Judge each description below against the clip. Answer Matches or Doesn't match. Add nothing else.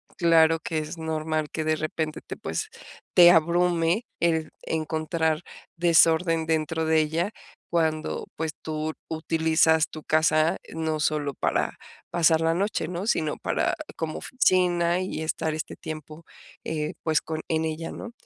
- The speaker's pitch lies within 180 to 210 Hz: Doesn't match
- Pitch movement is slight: Matches